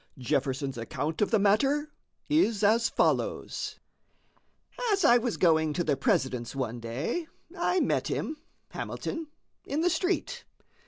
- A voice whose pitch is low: No, high, 210 Hz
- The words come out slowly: Yes, slow, 130 wpm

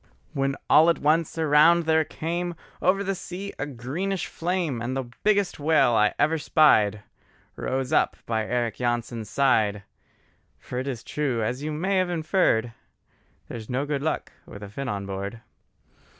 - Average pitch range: No, wide, 5.8 semitones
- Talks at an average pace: Yes, average, 160 wpm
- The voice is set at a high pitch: No, medium, 140 Hz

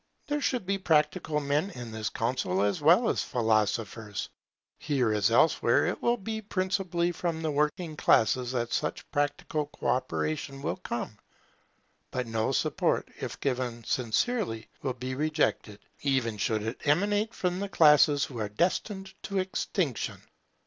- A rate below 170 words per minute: Yes, average, 150 wpm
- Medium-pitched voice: Yes, medium, 145 Hz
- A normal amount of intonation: No, wide, 7.4 semitones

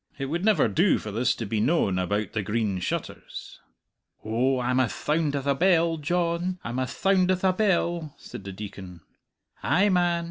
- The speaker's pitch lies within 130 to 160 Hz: Yes, medium, 140 Hz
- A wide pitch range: Yes, wide, 8.2 semitones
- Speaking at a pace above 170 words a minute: Yes, average, 185 wpm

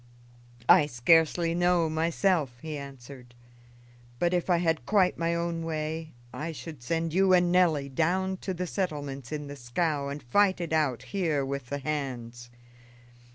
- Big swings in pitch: No, average, 3.8 semitones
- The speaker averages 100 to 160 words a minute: Yes, average, 155 wpm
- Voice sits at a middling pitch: Yes, medium, 155 Hz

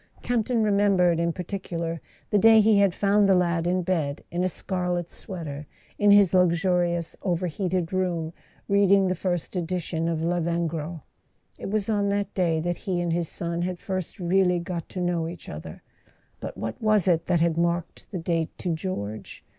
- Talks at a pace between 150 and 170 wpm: No, average, 180 wpm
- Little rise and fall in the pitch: Yes, narrow, 2.3 semitones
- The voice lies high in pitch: No, medium, 175 Hz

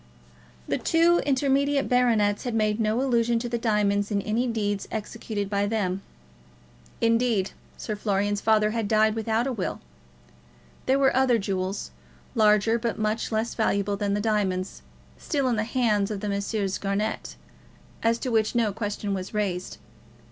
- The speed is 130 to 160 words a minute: Yes, average, 155 wpm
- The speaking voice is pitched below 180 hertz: No, high, 215 Hz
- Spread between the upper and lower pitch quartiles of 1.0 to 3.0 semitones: Yes, narrow, 2.5 semitones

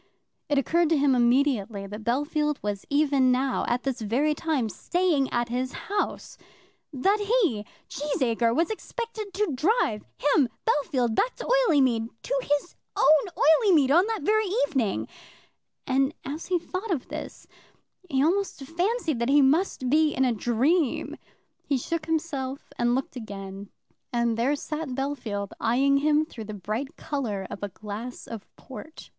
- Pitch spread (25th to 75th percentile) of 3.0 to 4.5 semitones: No, average, 5.2 semitones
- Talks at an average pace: Yes, average, 155 wpm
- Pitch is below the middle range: No, very high, 275 Hz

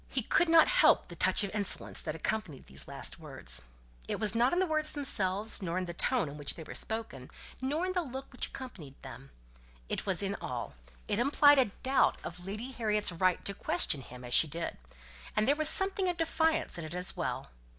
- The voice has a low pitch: No, high, 210 Hz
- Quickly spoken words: Yes, fast, 215 wpm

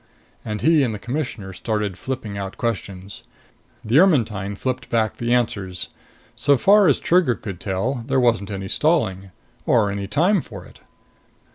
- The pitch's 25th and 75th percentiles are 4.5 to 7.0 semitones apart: Yes, average, 5.1 semitones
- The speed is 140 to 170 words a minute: Yes, average, 155 wpm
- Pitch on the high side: No, low, 115 Hz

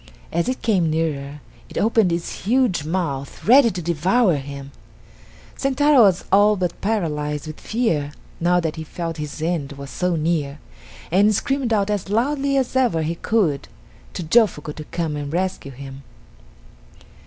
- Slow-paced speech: No, average, 155 wpm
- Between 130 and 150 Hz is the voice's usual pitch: No, medium, 175 Hz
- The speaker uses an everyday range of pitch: No, wide, 6.2 semitones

